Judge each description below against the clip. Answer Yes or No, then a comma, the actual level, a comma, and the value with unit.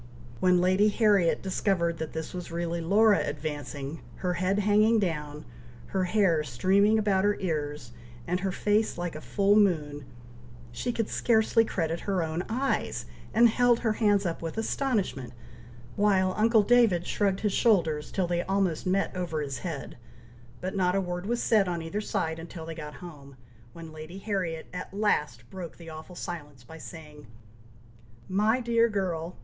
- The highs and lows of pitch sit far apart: No, average, 4.2 semitones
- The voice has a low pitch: No, medium, 180 Hz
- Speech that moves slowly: No, average, 165 wpm